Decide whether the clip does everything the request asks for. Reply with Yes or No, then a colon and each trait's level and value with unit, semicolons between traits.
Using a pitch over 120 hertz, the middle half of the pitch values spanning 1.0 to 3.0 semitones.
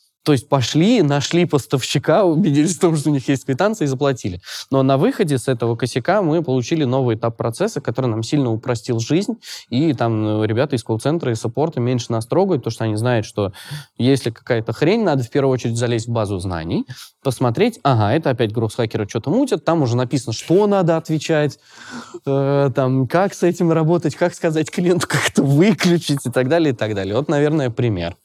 No: low, 135 Hz; average, 5.0 semitones